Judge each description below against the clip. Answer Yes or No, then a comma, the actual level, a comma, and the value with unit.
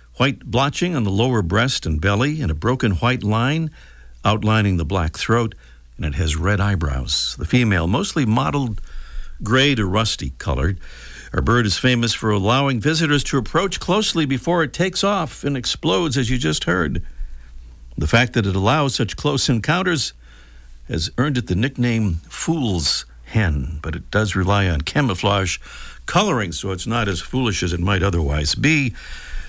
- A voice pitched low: Yes, low, 110 Hz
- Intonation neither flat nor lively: No, wide, 7.8 semitones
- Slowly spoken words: No, average, 165 wpm